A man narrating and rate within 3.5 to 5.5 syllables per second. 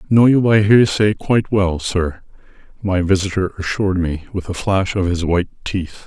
Yes: male; 5.1 syllables/s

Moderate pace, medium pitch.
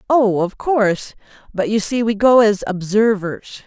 No: average, 165 wpm; high, 215 Hz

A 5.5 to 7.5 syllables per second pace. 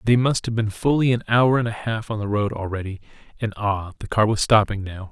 Yes: 5.7 syllables/s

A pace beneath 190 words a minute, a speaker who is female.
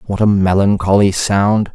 No: average, 140 wpm; male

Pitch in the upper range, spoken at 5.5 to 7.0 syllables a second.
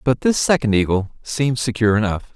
No: low, 120 Hz; 5.9 syllables/s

